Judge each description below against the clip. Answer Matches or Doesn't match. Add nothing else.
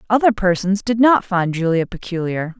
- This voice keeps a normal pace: Matches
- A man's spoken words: Doesn't match